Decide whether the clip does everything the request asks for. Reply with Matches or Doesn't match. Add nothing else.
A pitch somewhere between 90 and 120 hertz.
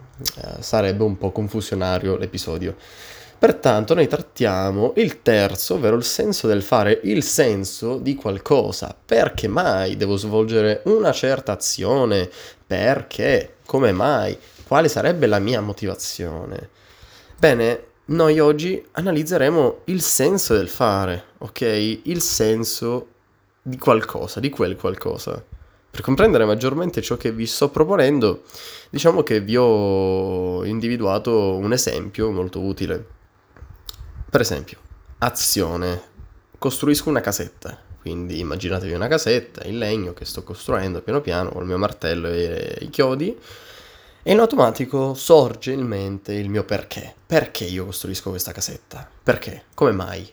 Matches